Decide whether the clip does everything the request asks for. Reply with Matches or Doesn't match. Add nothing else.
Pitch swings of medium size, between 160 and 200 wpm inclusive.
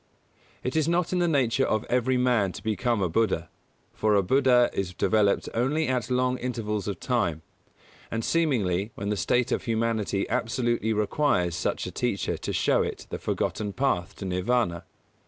Matches